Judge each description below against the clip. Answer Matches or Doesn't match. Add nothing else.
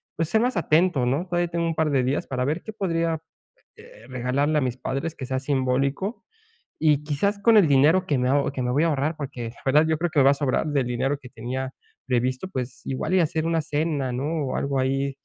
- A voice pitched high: Doesn't match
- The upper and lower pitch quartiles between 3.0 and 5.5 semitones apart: Matches